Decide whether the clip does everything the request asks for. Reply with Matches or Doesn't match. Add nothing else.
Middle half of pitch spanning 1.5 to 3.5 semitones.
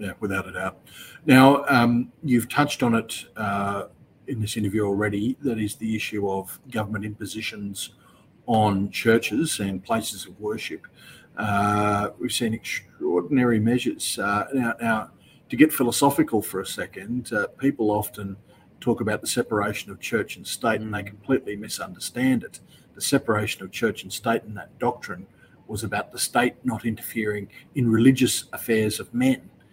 Matches